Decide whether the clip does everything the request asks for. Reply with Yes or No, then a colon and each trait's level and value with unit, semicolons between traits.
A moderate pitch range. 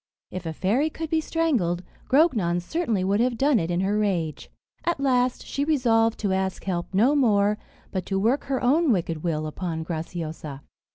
No: wide, 7.2 semitones